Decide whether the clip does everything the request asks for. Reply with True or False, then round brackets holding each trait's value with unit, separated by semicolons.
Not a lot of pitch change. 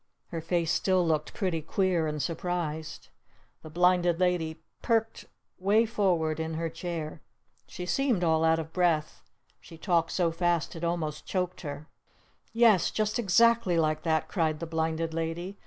True (2.3 semitones)